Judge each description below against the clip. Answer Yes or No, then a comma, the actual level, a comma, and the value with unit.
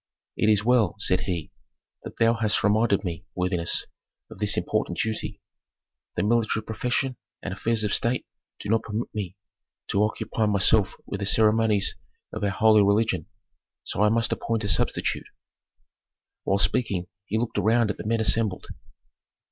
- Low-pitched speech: Yes, low, 105 Hz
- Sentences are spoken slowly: No, average, 155 wpm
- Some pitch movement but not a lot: No, narrow, 2.2 semitones